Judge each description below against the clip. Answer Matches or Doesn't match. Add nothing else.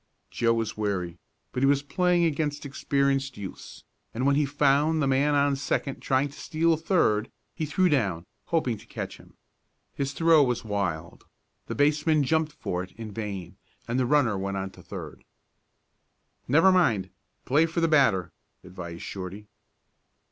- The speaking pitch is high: Doesn't match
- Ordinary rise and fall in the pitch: Doesn't match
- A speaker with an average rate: Matches